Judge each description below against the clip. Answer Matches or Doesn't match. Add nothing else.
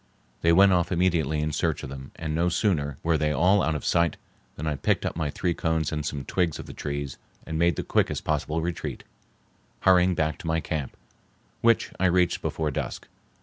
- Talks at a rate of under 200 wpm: Doesn't match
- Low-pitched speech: Matches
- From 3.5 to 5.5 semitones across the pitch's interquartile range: Doesn't match